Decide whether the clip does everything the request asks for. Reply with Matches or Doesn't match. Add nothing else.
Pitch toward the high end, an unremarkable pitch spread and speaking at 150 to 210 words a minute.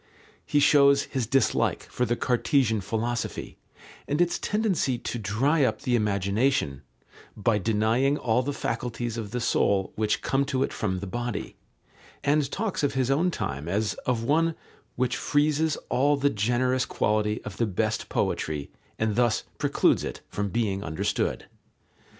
Doesn't match